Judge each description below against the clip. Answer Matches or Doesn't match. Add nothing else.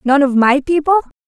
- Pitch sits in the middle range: Doesn't match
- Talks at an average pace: Matches